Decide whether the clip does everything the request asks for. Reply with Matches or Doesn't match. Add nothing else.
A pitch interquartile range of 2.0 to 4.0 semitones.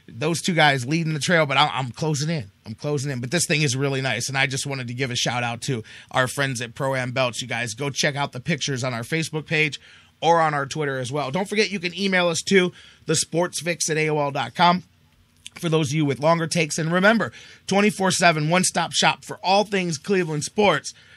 Doesn't match